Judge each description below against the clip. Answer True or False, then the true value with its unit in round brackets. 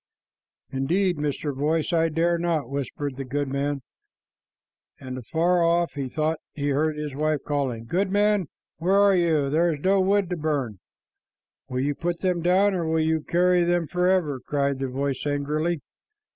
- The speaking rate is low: False (160 wpm)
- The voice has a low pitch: False (155 Hz)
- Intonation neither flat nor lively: True (3.7 semitones)